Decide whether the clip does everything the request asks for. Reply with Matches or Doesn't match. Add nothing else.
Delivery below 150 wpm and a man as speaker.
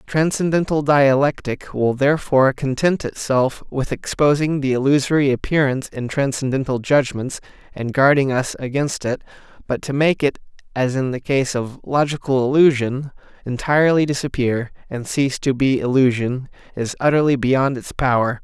Matches